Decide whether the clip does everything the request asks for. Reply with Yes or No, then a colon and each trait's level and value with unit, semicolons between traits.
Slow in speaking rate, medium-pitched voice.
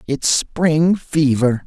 Yes: slow, 110 wpm; medium, 145 Hz